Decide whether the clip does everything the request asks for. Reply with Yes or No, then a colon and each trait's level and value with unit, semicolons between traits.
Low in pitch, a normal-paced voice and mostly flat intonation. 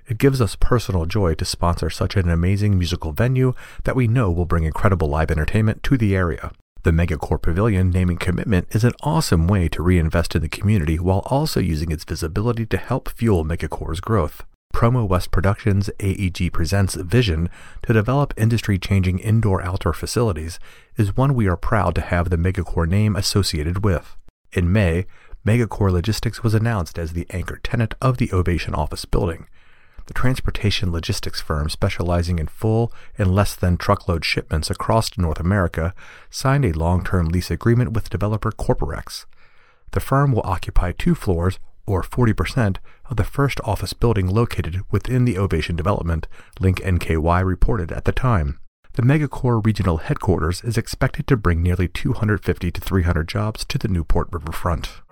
No: very low, 95 Hz; average, 165 wpm; average, 4.3 semitones